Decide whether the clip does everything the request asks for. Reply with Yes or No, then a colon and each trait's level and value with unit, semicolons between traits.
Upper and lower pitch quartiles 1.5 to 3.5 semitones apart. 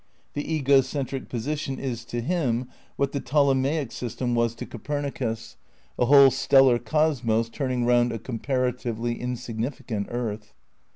Yes: average, 2.9 semitones